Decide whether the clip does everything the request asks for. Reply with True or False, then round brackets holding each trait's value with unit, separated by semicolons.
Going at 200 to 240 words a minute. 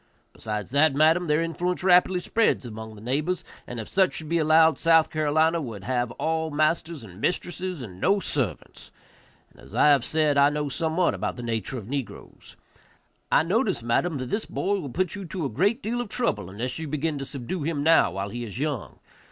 True (205 wpm)